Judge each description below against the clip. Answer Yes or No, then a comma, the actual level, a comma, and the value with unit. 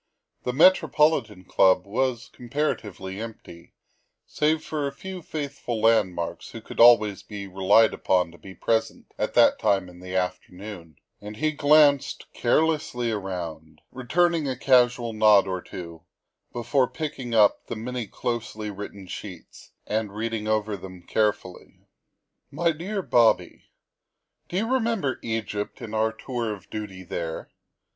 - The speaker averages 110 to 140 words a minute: Yes, slow, 135 wpm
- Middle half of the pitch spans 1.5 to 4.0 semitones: No, wide, 5.6 semitones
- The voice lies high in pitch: No, low, 110 Hz